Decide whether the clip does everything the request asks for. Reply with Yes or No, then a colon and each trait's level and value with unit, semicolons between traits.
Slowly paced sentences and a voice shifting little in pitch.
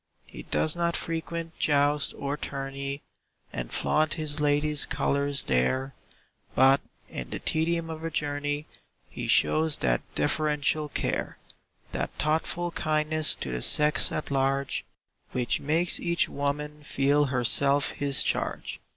Yes: slow, 130 wpm; narrow, 2.1 semitones